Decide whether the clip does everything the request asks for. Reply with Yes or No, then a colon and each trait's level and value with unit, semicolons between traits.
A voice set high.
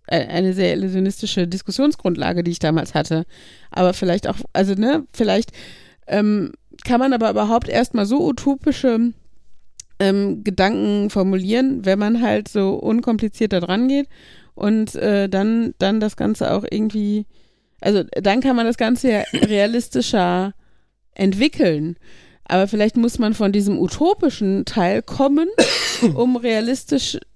Yes: high, 210 Hz